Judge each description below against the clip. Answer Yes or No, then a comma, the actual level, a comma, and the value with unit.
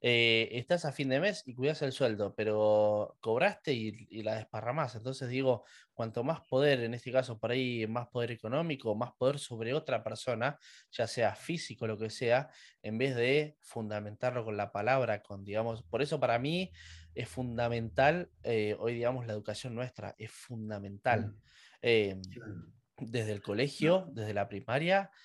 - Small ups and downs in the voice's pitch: No, average, 3.6 semitones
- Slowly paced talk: No, average, 165 wpm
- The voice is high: No, low, 120 Hz